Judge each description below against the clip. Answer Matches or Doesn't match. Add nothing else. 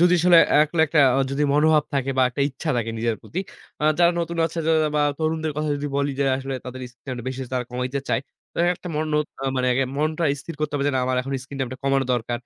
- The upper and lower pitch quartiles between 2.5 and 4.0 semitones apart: Matches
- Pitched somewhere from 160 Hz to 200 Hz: Doesn't match